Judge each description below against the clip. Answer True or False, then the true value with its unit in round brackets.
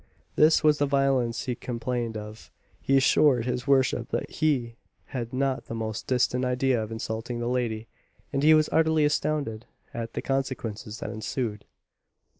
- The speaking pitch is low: True (125 Hz)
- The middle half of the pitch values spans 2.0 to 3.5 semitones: True (3.1 semitones)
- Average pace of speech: True (160 wpm)